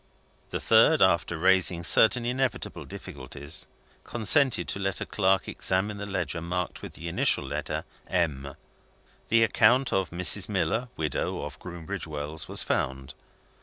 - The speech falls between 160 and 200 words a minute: No, average, 140 wpm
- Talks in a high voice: No, very low, 95 Hz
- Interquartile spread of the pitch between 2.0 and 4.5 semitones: No, average, 5.3 semitones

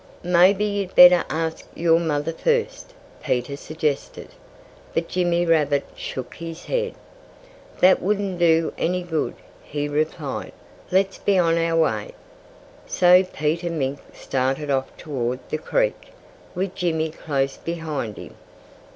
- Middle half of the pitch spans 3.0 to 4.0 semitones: Yes, average, 3.4 semitones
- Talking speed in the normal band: No, slow, 125 wpm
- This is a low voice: No, medium, 165 Hz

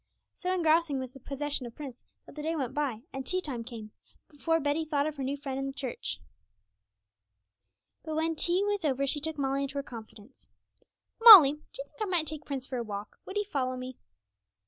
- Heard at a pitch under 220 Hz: No, very high, 285 Hz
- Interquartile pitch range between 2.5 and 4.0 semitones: Yes, average, 3.5 semitones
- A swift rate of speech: Yes, fast, 215 wpm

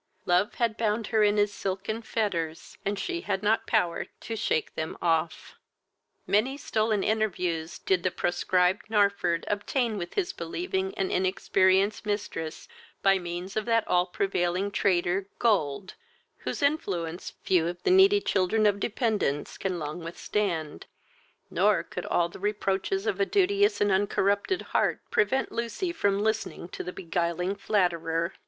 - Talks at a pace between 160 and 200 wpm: No, average, 150 wpm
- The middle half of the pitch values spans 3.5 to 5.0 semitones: Yes, average, 3.8 semitones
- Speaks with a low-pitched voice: No, high, 200 Hz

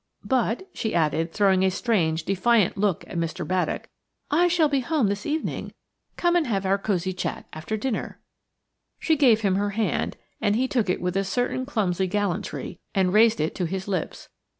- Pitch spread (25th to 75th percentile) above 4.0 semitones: Yes, average, 4.6 semitones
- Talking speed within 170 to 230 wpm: Yes, average, 190 wpm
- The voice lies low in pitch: No, high, 200 Hz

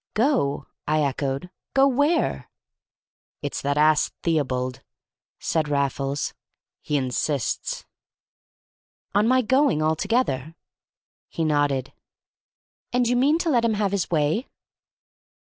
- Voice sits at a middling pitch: Yes, medium, 155 Hz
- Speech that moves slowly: Yes, slow, 110 wpm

